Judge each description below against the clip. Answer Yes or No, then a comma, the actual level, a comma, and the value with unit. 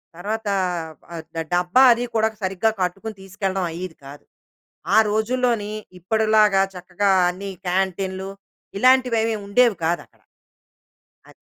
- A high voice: Yes, high, 200 Hz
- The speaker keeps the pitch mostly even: No, average, 3.2 semitones